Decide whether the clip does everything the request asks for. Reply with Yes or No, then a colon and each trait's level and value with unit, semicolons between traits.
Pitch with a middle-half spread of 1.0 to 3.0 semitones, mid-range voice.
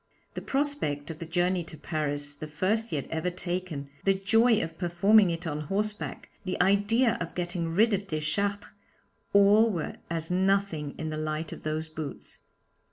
No: average, 4.3 semitones; medium, 175 Hz